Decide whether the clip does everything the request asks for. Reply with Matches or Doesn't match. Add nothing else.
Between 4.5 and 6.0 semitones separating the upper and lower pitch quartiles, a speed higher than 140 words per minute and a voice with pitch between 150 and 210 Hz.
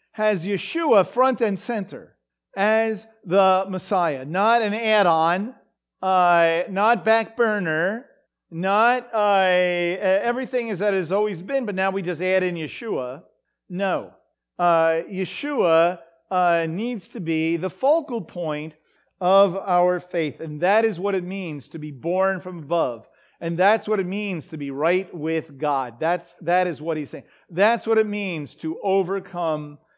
Doesn't match